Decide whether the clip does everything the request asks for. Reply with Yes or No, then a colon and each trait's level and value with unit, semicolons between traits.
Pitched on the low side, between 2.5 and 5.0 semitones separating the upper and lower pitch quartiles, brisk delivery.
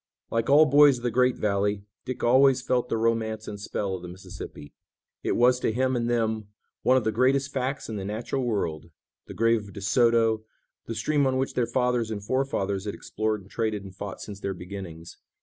Yes: low, 115 Hz; average, 3.8 semitones; fast, 210 wpm